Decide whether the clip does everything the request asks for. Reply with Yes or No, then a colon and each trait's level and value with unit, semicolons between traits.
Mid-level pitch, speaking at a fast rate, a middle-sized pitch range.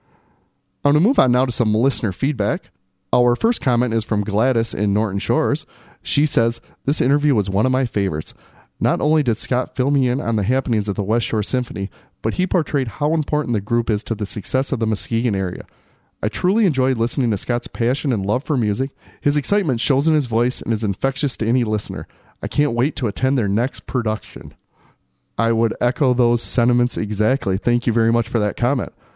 No: low, 120 Hz; fast, 210 wpm; average, 3.8 semitones